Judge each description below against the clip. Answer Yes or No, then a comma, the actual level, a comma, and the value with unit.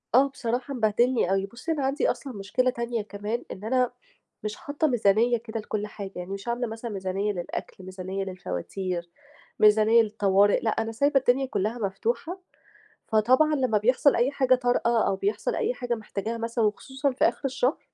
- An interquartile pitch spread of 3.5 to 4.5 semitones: Yes, average, 4.0 semitones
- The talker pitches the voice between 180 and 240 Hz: Yes, high, 230 Hz